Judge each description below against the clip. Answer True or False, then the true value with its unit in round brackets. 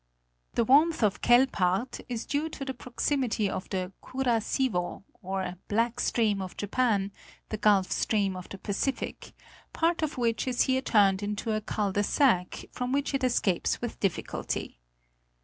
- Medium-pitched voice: False (225 Hz)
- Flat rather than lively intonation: False (4.8 semitones)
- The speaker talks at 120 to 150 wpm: False (160 wpm)